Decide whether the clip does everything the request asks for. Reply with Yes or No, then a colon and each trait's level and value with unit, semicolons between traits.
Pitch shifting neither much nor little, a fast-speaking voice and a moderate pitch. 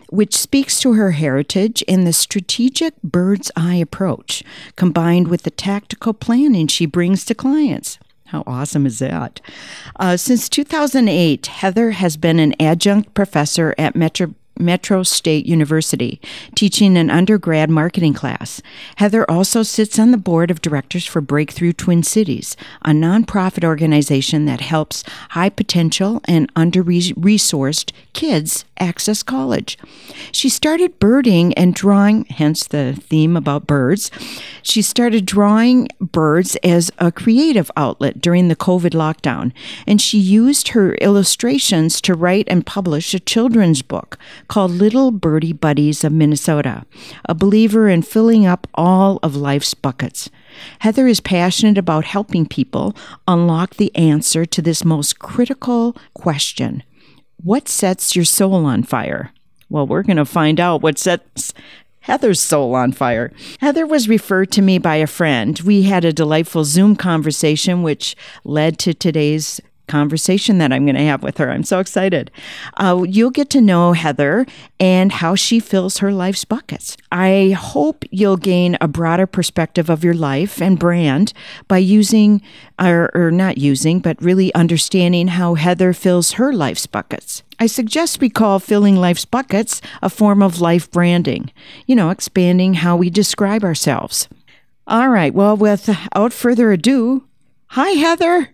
No: average, 4.6 semitones; average, 150 wpm; medium, 180 Hz